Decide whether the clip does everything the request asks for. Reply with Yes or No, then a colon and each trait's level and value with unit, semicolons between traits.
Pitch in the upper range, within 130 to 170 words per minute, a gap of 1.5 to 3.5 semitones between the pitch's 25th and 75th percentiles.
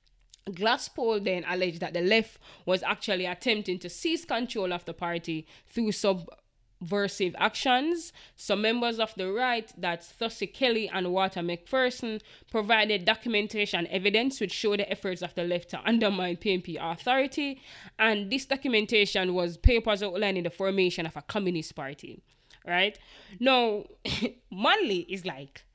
No: high, 195 Hz; average, 140 wpm; average, 4.2 semitones